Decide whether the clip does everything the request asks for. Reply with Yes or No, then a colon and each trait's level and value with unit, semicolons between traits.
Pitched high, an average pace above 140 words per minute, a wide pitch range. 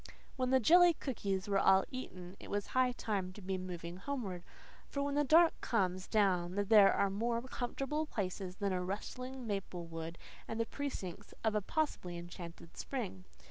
Yes: high, 200 Hz; average, 175 wpm; wide, 5.8 semitones